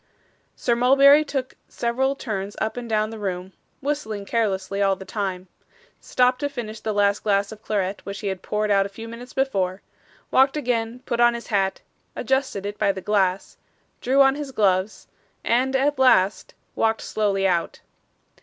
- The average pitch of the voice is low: No, high, 220 Hz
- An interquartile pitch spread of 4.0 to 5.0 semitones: Yes, average, 4.3 semitones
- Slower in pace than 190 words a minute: Yes, average, 175 wpm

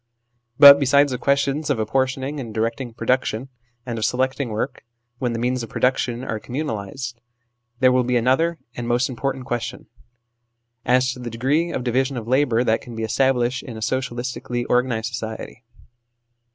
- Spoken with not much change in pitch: Yes, narrow, 2.2 semitones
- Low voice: Yes, low, 125 Hz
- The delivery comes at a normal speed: Yes, average, 165 wpm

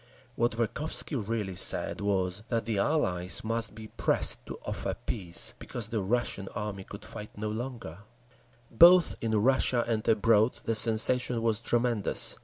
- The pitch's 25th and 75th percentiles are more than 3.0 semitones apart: No, narrow, 2.5 semitones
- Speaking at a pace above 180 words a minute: No, average, 150 wpm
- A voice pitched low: Yes, low, 110 Hz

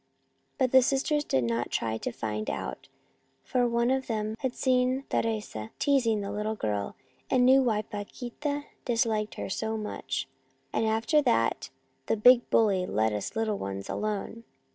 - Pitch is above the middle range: Yes, high, 220 Hz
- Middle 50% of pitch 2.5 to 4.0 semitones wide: No, average, 4.6 semitones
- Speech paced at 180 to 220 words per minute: No, average, 160 wpm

